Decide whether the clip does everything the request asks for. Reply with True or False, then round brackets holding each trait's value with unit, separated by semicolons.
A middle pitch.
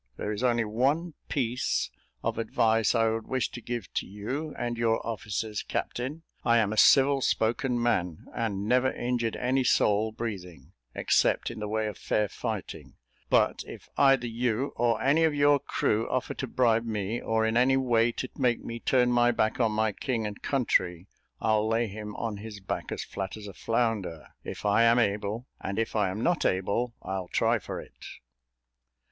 False (115 Hz)